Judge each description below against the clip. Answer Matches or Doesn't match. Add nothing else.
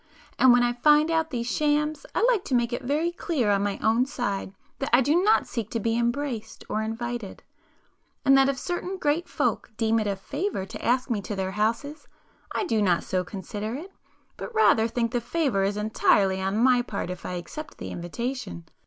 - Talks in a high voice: Matches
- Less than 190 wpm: Doesn't match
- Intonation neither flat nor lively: Doesn't match